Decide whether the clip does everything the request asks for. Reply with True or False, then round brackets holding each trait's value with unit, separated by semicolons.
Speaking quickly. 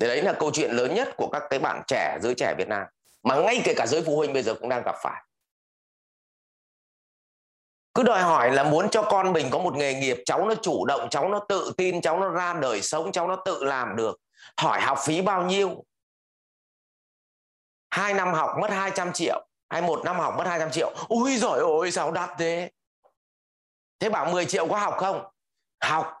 True (210 wpm)